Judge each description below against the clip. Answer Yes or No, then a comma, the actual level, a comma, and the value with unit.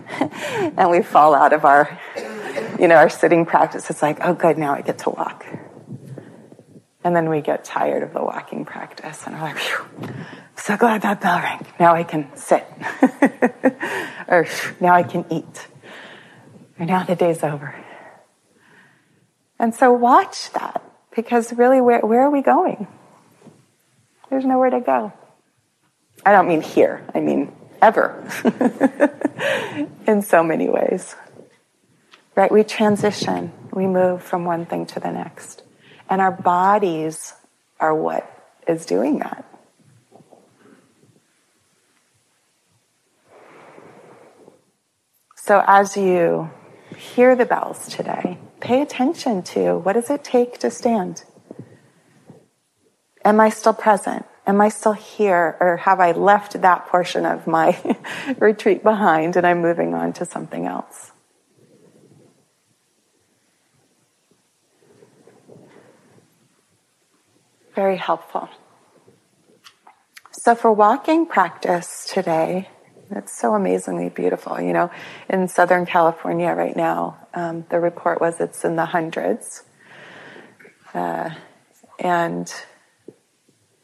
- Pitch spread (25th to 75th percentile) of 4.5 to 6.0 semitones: Yes, average, 5.2 semitones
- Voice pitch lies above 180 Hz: Yes, high, 190 Hz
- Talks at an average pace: No, slow, 120 wpm